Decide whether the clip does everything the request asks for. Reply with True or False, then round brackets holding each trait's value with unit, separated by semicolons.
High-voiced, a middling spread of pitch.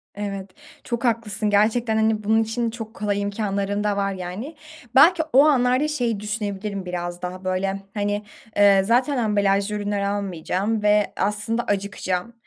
False (205 Hz; 2.3 semitones)